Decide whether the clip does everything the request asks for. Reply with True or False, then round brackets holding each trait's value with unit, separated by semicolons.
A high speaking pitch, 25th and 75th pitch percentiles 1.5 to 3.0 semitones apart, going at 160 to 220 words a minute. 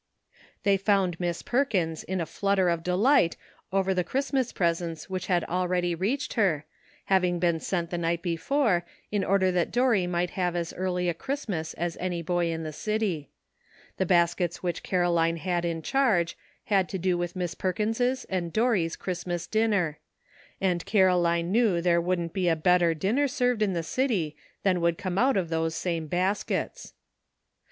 False (180 Hz; 2.7 semitones; 180 wpm)